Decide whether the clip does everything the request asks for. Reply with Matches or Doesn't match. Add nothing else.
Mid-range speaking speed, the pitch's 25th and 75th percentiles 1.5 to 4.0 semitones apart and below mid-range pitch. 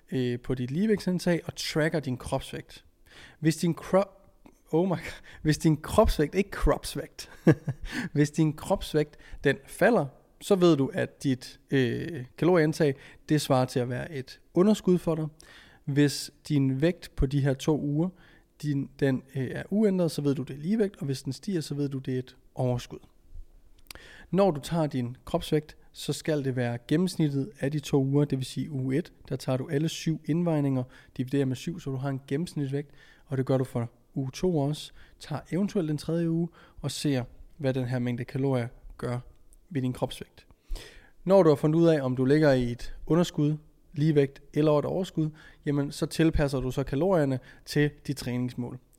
Doesn't match